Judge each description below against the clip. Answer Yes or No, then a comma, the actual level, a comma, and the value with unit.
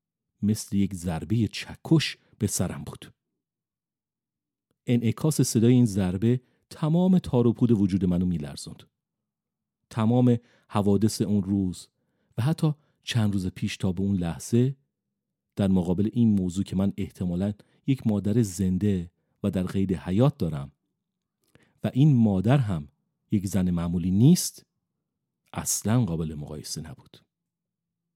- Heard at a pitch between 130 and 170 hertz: No, low, 105 Hz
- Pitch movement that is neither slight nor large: Yes, average, 4.8 semitones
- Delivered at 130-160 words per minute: No, average, 120 wpm